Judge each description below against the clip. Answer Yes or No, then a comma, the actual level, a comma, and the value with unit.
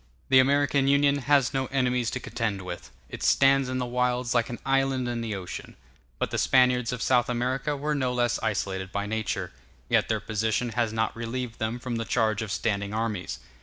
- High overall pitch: No, low, 120 Hz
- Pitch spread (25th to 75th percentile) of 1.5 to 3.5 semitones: Yes, average, 2.8 semitones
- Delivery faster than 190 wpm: Yes, average, 200 wpm